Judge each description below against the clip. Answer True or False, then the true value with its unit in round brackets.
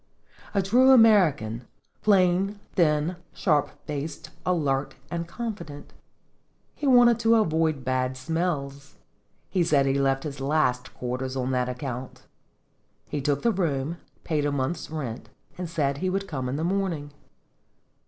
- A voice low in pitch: False (150 Hz)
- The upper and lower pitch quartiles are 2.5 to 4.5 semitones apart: False (5.2 semitones)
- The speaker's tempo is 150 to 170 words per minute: False (140 wpm)